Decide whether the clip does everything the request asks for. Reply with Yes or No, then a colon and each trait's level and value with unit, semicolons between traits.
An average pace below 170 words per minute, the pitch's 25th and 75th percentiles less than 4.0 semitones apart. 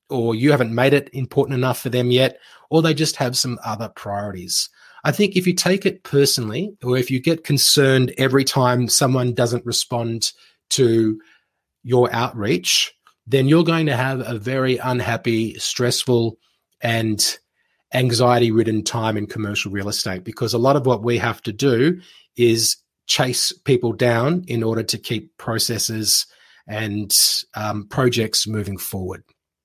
Yes: average, 155 wpm; average, 2.9 semitones